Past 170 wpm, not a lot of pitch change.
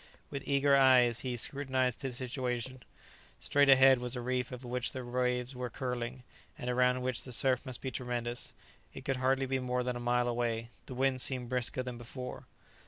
Yes: average, 190 wpm; narrow, 1.1 semitones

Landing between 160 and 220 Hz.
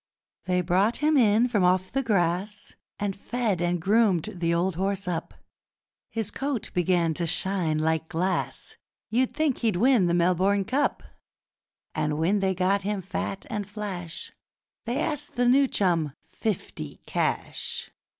Yes: high, 190 Hz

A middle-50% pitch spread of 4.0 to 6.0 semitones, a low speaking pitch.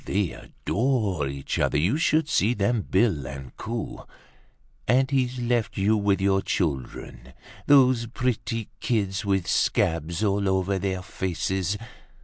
Yes: average, 4.5 semitones; low, 100 Hz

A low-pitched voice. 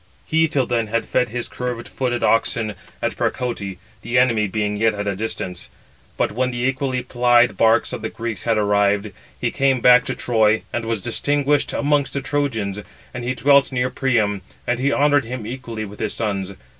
Yes: low, 120 Hz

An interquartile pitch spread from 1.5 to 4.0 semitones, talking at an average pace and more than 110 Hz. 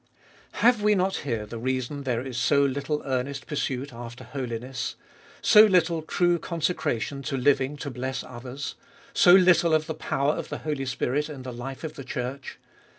Yes: average, 3.7 semitones; average, 180 wpm; medium, 140 Hz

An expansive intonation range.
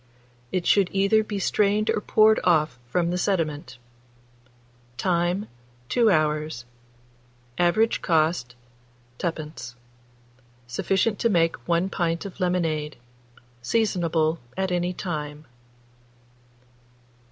No: average, 4.0 semitones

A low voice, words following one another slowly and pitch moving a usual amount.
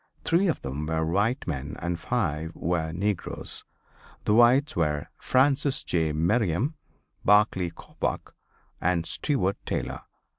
No: very low, 90 Hz; slow, 120 wpm; wide, 6.8 semitones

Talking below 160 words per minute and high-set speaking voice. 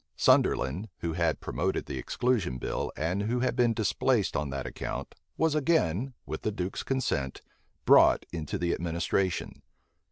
No: average, 150 wpm; very low, 95 Hz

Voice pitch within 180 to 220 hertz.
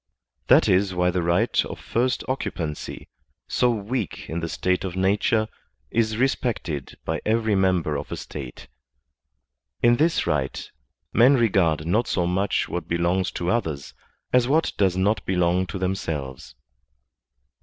No: very low, 95 Hz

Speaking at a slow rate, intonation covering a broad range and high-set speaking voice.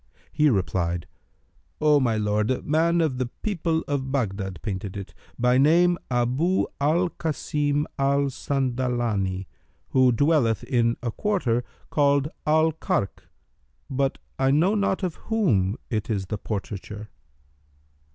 No: slow, 130 wpm; wide, 6.1 semitones; low, 130 Hz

